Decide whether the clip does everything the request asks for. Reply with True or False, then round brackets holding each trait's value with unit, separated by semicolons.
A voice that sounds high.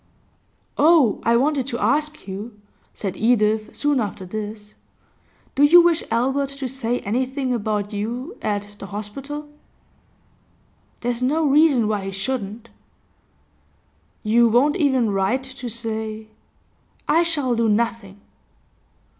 True (235 Hz)